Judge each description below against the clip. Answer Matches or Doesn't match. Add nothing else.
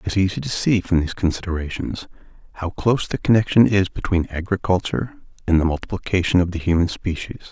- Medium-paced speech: Matches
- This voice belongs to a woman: Doesn't match